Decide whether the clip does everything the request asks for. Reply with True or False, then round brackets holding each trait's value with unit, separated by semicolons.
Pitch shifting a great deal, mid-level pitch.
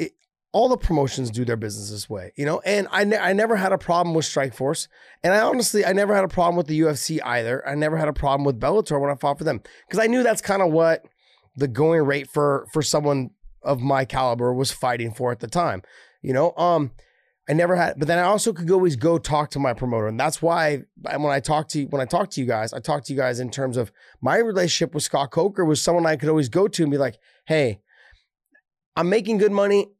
False (4.5 semitones; 155 Hz)